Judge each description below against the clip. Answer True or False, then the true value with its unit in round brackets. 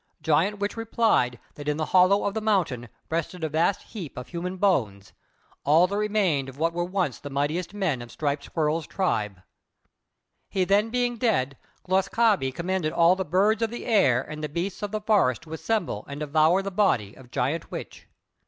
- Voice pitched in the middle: True (170 Hz)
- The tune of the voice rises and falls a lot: True (5.8 semitones)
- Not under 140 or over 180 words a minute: False (190 wpm)